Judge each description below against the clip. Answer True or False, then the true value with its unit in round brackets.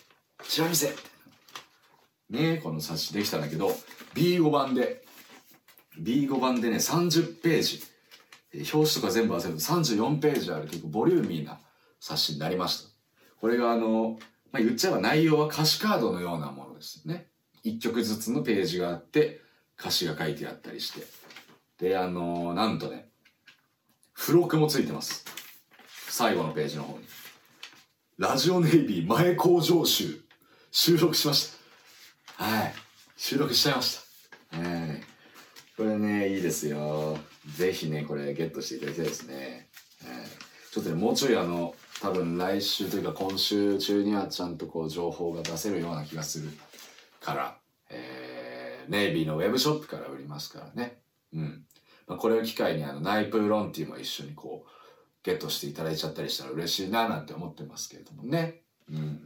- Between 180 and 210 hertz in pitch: False (105 Hz)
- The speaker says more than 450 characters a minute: False (335 characters per minute)